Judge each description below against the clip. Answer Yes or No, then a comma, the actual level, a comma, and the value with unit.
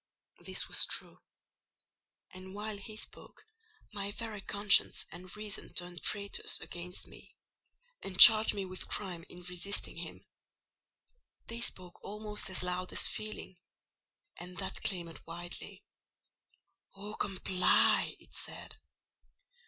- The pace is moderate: No, slow, 120 wpm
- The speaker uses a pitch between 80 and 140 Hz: No, high, 190 Hz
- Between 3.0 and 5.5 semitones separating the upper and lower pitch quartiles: No, narrow, 2.6 semitones